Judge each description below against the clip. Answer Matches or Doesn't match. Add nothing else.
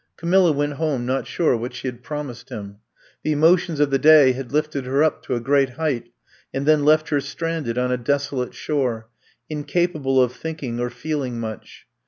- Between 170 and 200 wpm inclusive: Matches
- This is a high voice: Doesn't match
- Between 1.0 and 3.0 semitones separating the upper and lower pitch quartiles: Doesn't match